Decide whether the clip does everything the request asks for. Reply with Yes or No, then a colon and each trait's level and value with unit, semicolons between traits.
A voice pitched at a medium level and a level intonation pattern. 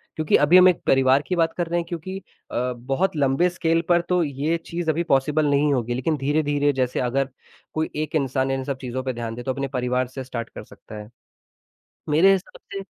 No: medium, 145 Hz; average, 4.1 semitones